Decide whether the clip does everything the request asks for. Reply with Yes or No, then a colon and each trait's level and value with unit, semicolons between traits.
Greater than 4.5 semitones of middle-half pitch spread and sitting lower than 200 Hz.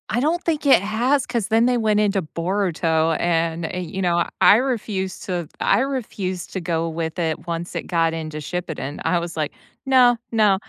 Yes: average, 5.3 semitones; medium, 185 Hz